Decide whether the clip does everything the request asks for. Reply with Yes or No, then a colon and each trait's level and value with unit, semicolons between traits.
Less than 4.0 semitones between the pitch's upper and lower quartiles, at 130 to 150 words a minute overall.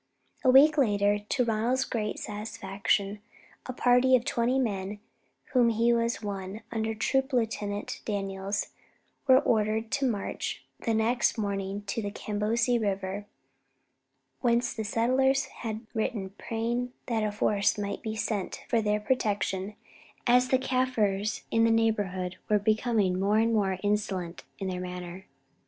Yes: average, 2.8 semitones; average, 145 wpm